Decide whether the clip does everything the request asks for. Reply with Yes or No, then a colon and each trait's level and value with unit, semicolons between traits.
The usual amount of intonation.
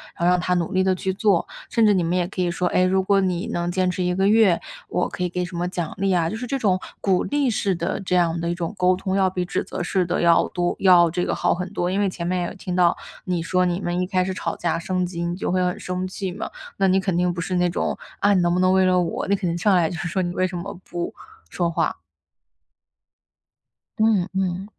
No: narrow, 1.5 semitones